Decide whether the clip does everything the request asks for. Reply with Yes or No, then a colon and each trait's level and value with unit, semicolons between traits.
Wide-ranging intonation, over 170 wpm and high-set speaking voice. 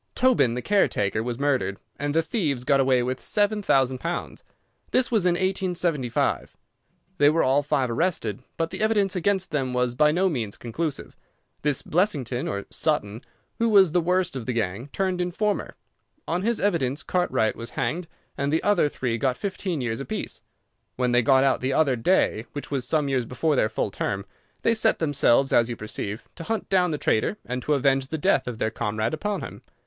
No: wide, 6.5 semitones; average, 195 wpm; medium, 145 Hz